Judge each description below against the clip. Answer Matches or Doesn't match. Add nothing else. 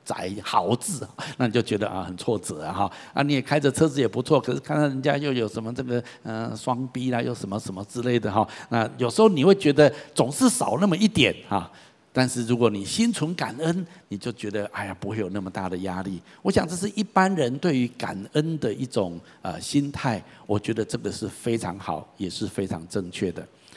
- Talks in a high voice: Doesn't match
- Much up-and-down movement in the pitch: Matches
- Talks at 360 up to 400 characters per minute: Doesn't match